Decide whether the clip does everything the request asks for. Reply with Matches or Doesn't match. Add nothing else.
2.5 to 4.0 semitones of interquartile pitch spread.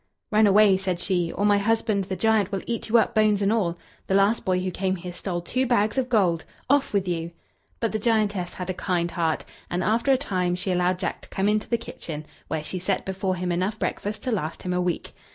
Matches